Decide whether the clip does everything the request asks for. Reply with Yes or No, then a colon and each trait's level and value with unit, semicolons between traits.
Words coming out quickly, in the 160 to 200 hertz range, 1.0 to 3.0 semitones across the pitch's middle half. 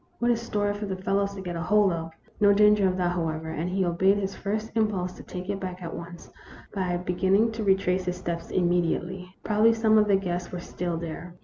Yes: fast, 220 wpm; medium, 185 Hz; narrow, 2.6 semitones